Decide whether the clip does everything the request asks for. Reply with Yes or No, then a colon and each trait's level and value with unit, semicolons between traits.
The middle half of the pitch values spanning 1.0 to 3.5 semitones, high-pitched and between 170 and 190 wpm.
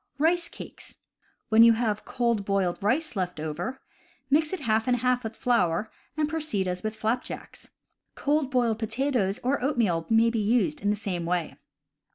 No: average, 4.6 semitones; high, 230 Hz; average, 175 wpm